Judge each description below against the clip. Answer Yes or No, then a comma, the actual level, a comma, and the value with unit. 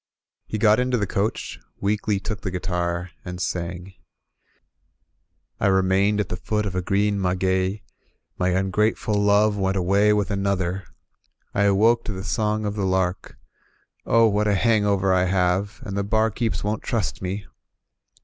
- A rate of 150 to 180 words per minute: Yes, average, 155 wpm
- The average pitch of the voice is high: No, low, 100 Hz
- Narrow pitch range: Yes, narrow, 2.2 semitones